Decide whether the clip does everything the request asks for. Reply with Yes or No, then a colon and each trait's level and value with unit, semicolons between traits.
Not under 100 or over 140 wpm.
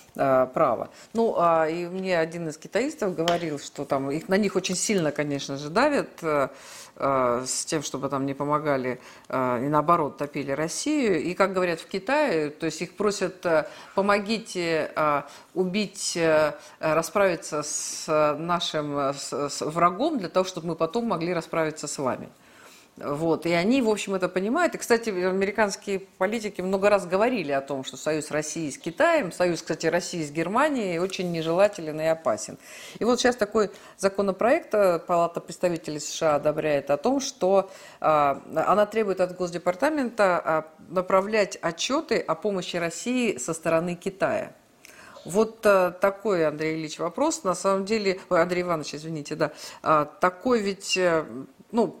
No: average, 150 wpm